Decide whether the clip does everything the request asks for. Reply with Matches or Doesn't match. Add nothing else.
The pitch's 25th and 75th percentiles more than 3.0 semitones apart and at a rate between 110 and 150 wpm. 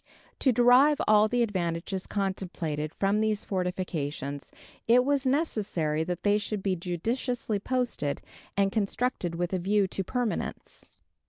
Matches